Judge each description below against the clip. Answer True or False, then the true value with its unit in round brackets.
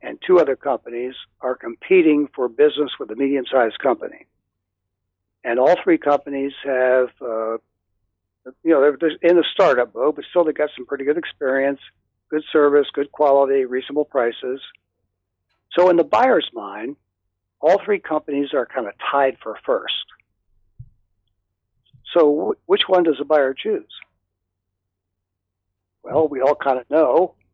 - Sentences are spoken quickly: False (145 wpm)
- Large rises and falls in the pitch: True (7.4 semitones)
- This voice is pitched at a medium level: False (130 Hz)